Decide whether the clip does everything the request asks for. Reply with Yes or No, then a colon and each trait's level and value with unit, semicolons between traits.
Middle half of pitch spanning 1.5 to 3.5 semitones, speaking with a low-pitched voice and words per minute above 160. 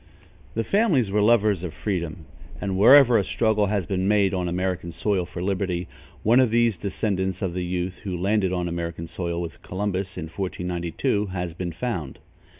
Yes: average, 3.0 semitones; very low, 95 Hz; average, 175 wpm